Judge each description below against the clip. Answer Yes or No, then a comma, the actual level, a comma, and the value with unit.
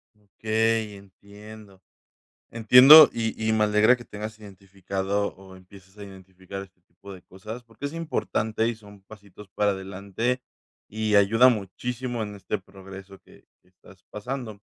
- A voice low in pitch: Yes, low, 105 Hz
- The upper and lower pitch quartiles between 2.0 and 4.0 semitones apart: Yes, narrow, 2.4 semitones